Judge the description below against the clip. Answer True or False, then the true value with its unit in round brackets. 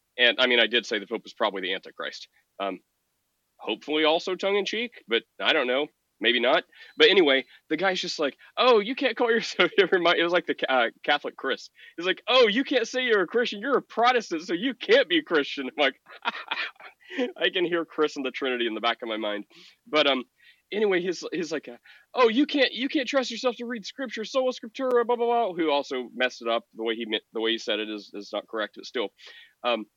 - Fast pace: True (235 wpm)